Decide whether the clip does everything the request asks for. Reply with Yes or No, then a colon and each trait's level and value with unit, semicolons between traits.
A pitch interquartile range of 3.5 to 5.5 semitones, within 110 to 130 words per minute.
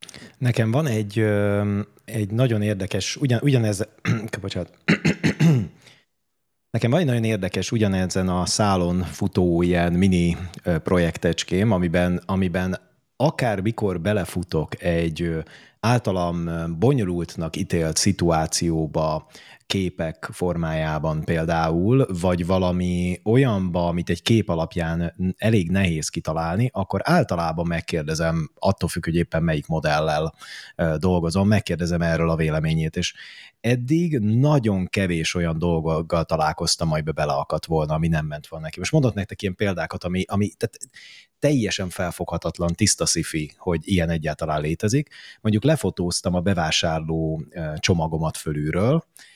Yes: average, 4.1 semitones; average, 120 wpm